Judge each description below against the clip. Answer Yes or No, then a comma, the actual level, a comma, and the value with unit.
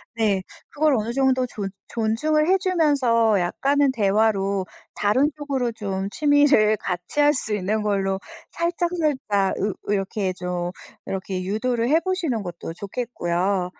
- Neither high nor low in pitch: No, high, 220 Hz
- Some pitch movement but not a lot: No, wide, 6.7 semitones